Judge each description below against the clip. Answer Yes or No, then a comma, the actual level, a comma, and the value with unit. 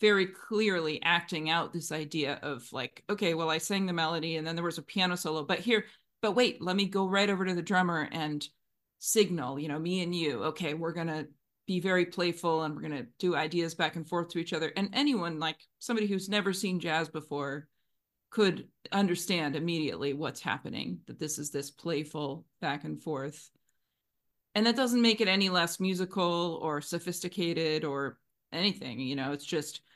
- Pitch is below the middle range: No, medium, 170 Hz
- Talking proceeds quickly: No, average, 195 wpm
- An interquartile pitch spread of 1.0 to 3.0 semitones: No, average, 3.5 semitones